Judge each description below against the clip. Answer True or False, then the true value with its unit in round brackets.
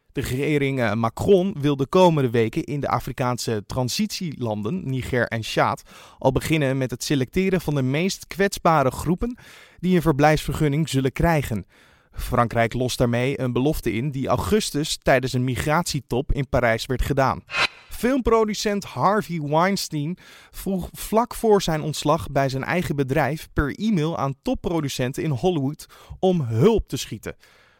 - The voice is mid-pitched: True (145 Hz)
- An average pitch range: False (5.8 semitones)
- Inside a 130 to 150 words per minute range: True (140 wpm)